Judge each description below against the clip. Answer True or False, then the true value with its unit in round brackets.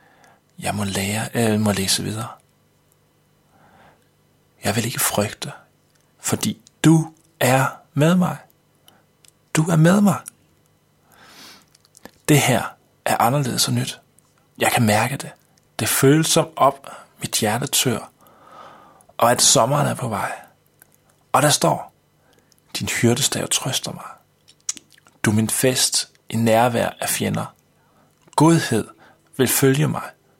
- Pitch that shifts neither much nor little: False (6.0 semitones)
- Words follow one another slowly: True (120 wpm)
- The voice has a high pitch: False (135 Hz)